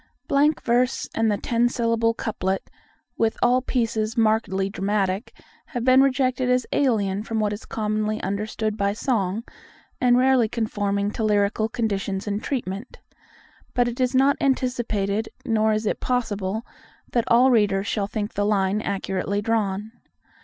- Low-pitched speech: No, high, 220 Hz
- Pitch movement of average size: Yes, average, 3.1 semitones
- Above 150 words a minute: No, average, 145 wpm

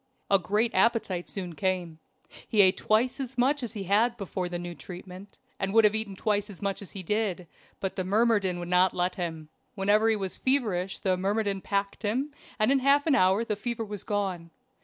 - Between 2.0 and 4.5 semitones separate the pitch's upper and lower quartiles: Yes, average, 3.3 semitones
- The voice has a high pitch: Yes, high, 200 Hz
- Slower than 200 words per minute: No, fast, 205 wpm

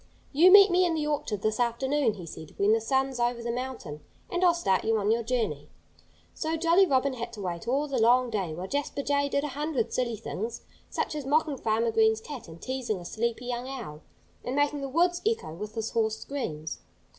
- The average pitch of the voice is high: Yes, high, 245 Hz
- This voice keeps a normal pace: No, fast, 215 wpm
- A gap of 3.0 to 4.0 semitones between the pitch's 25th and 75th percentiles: No, average, 4.8 semitones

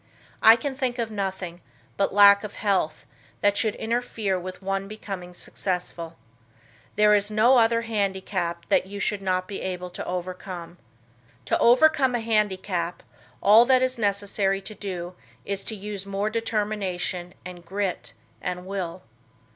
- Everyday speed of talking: Yes, average, 150 wpm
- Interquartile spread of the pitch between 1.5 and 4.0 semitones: Yes, average, 2.9 semitones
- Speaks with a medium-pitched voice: No, high, 195 Hz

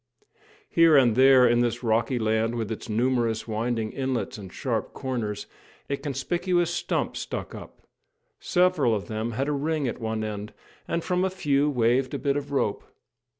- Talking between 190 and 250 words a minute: No, average, 170 wpm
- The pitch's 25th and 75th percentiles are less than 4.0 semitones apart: No, average, 4.3 semitones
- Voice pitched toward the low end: Yes, low, 125 Hz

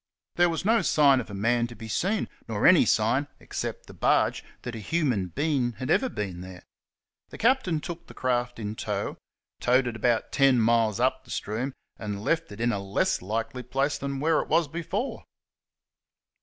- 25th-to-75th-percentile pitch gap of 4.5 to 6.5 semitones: Yes, average, 5.3 semitones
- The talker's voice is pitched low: Yes, low, 125 Hz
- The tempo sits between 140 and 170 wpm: No, average, 190 wpm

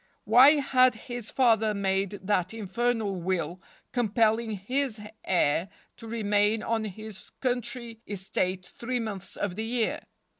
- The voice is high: Yes, high, 220 Hz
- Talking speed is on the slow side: Yes, slow, 125 wpm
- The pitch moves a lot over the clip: No, average, 3.6 semitones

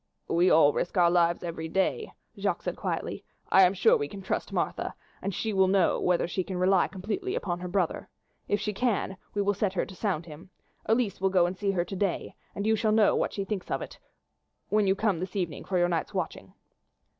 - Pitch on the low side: No, high, 190 Hz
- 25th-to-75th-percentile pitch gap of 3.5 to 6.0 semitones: No, narrow, 2.5 semitones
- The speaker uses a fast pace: Yes, fast, 225 wpm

